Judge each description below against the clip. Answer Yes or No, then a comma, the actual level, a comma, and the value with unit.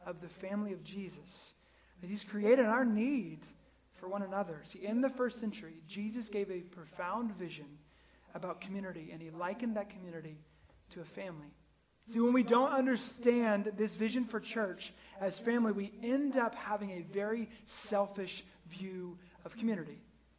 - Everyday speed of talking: Yes, average, 160 wpm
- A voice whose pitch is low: No, high, 200 Hz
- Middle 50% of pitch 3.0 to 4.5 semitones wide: Yes, average, 4.1 semitones